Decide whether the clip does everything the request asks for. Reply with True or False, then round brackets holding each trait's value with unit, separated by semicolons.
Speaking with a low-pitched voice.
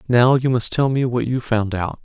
True (120 Hz)